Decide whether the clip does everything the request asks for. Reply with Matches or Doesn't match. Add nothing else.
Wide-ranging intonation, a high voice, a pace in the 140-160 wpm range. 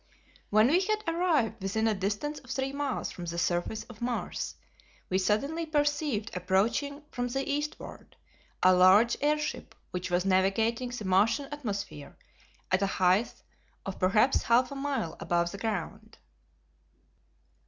Matches